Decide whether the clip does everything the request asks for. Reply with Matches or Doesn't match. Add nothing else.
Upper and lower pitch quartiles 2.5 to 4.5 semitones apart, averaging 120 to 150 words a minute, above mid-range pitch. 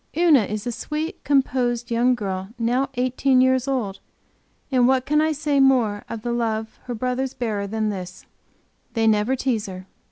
Doesn't match